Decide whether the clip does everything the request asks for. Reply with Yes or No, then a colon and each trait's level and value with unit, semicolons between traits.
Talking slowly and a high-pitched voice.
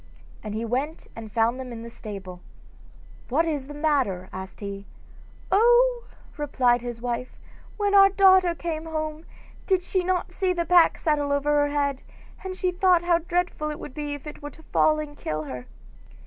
No: average, 185 wpm; very high, 295 Hz